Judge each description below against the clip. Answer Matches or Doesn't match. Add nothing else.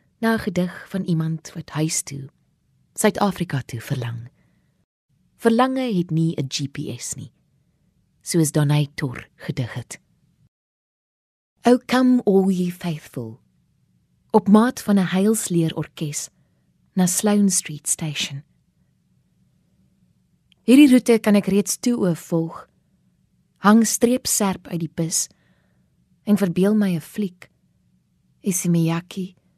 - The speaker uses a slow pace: Matches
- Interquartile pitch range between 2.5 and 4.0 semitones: Doesn't match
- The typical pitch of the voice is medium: Matches